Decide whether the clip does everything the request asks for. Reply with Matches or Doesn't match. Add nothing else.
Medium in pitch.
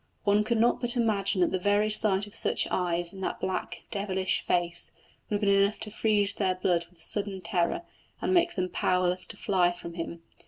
Doesn't match